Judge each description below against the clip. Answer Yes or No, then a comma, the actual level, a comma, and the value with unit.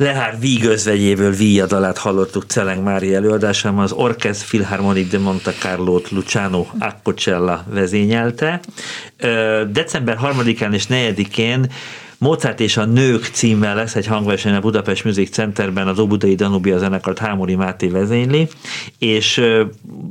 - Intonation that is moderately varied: Yes, average, 3.2 semitones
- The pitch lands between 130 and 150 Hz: No, low, 110 Hz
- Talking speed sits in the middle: Yes, average, 120 wpm